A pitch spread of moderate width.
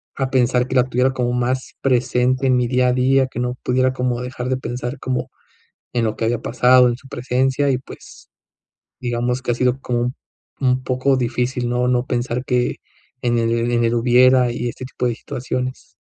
No: narrow, 1.1 semitones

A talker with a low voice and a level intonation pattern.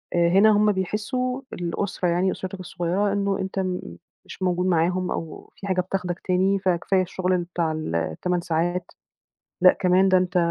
No: medium, 185 Hz; narrow, 1.7 semitones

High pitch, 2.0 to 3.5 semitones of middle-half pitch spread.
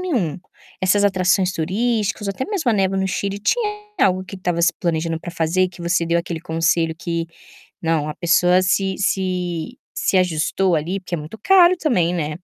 No: medium, 180 Hz; average, 2.7 semitones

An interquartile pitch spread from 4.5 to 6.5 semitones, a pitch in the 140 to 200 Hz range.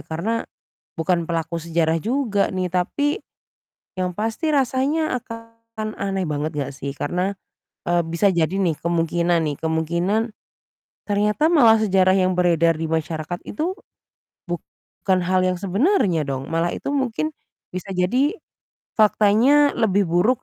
Yes: average, 5.2 semitones; medium, 185 Hz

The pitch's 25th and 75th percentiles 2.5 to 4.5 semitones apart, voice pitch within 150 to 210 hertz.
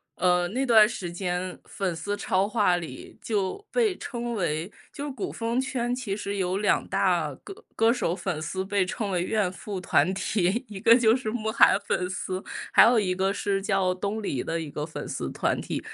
Yes: average, 3.6 semitones; high, 195 Hz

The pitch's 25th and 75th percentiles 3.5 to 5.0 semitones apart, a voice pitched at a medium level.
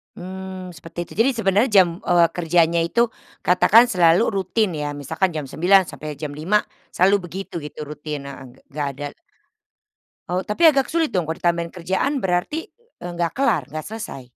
Yes: average, 4.1 semitones; medium, 180 Hz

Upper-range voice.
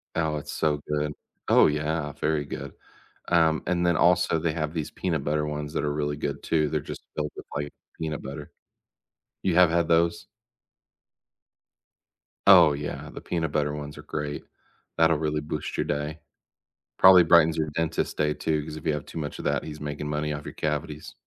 No: very low, 75 Hz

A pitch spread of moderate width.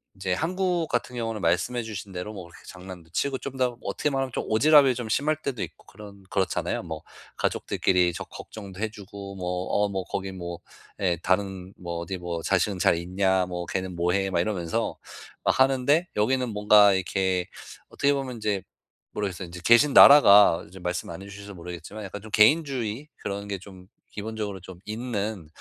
Yes: average, 4.3 semitones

